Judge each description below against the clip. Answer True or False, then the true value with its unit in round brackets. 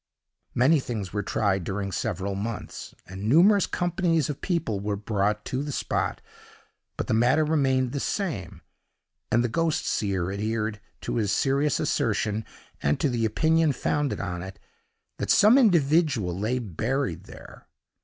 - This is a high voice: False (115 Hz)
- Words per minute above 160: False (150 wpm)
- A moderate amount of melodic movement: False (6.7 semitones)